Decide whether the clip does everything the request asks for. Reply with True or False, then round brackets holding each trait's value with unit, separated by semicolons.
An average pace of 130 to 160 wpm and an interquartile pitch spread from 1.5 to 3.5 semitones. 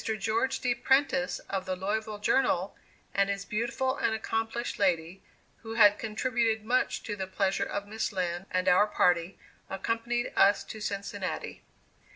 True (150 wpm; 3.0 semitones)